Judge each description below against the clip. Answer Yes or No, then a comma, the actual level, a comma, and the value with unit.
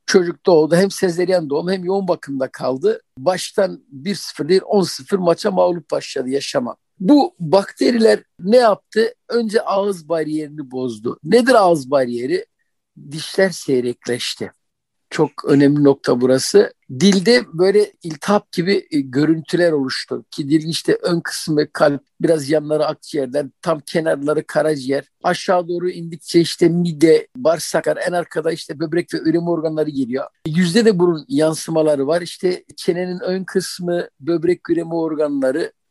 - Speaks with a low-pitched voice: No, medium, 170 Hz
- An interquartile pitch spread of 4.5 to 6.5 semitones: No, average, 3.9 semitones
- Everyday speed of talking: Yes, average, 130 wpm